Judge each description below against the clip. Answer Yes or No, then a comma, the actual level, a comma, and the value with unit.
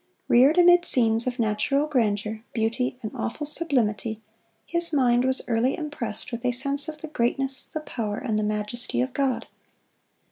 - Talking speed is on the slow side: No, average, 165 wpm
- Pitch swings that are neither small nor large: Yes, average, 4.2 semitones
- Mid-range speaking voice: No, very high, 250 Hz